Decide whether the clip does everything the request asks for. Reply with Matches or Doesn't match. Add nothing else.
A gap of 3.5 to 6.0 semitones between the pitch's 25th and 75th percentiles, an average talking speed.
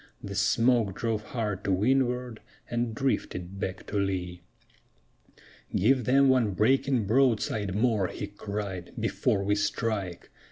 Doesn't match